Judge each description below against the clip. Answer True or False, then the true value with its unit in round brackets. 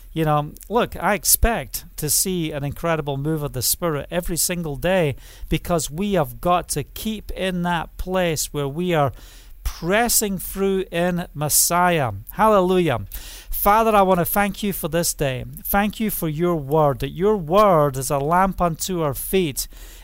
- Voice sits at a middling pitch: True (170 Hz)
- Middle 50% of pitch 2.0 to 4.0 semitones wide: False (4.4 semitones)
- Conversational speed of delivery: True (170 wpm)